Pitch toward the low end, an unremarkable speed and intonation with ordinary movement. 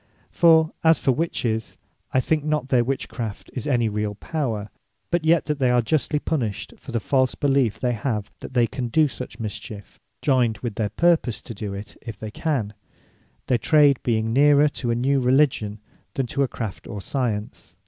Yes: low, 125 Hz; average, 195 wpm; average, 4.6 semitones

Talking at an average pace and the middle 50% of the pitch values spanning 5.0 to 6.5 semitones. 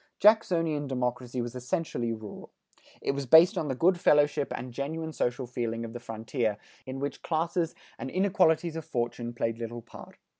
Yes: average, 165 wpm; average, 5.3 semitones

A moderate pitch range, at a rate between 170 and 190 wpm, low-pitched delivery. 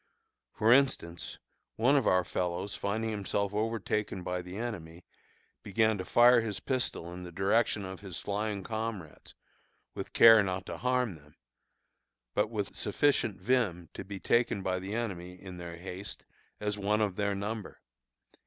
No: average, 3.5 semitones; average, 155 wpm; low, 100 Hz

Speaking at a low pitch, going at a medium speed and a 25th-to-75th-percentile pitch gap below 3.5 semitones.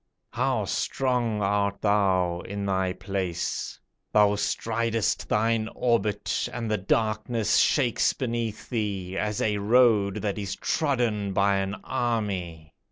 No: low, 105 Hz; slow, 120 wpm; average, 2.7 semitones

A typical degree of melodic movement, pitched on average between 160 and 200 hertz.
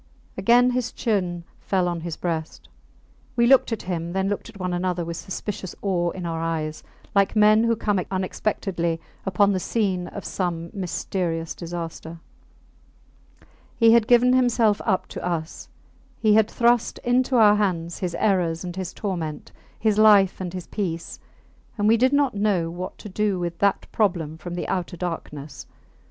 Yes: average, 3.9 semitones; medium, 185 Hz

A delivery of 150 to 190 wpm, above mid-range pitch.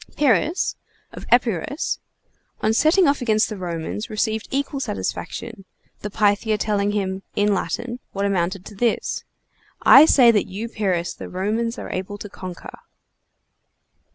No: average, 140 wpm; high, 210 Hz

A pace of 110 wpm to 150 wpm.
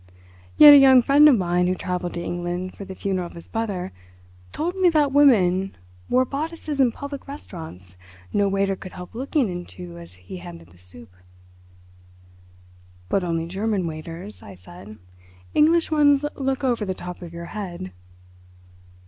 No: average, 160 wpm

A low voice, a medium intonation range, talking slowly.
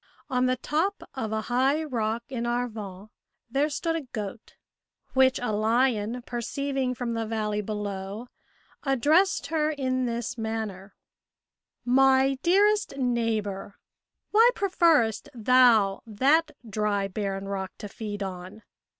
No: high, 240 Hz; average, 4.2 semitones; slow, 125 wpm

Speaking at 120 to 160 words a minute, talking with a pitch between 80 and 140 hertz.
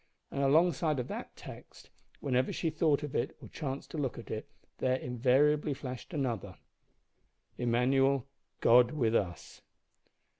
Yes: average, 140 wpm; low, 135 Hz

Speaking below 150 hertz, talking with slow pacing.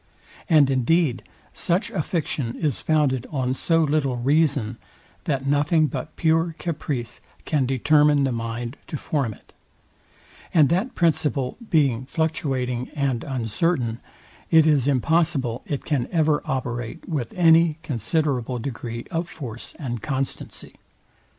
Yes: medium, 140 Hz; slow, 125 wpm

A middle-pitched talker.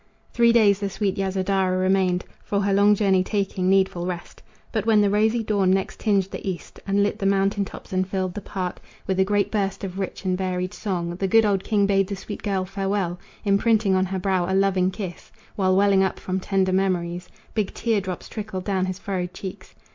No: high, 195 Hz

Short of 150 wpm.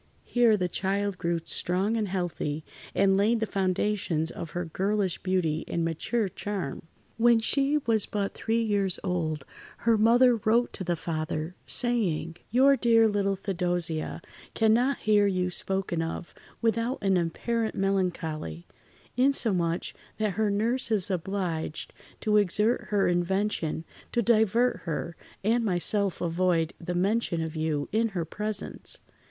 Yes: average, 140 wpm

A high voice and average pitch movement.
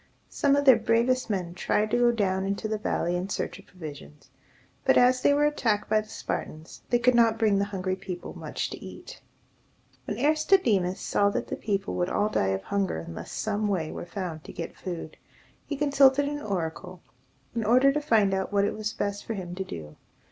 Yes: high, 205 Hz; average, 4.7 semitones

